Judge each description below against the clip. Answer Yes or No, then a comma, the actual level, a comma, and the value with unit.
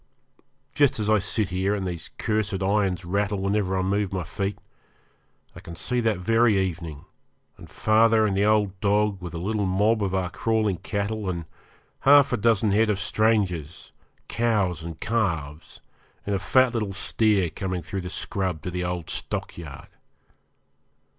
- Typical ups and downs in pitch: Yes, average, 3.1 semitones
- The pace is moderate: Yes, average, 165 wpm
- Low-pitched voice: Yes, low, 100 Hz